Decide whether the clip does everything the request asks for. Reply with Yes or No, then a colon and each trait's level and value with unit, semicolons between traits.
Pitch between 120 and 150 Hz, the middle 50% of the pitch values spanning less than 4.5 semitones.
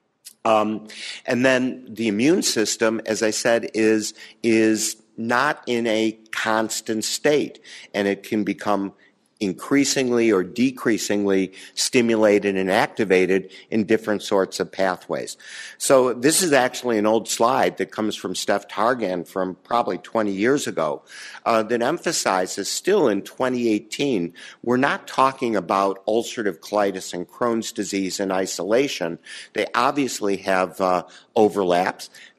No: low, 110 Hz; average, 3.1 semitones